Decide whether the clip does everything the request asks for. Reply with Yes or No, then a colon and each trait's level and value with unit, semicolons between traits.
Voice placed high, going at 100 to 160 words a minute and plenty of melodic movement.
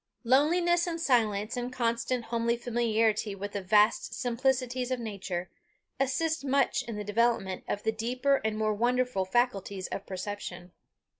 No: high, 235 Hz; average, 145 wpm; average, 3.6 semitones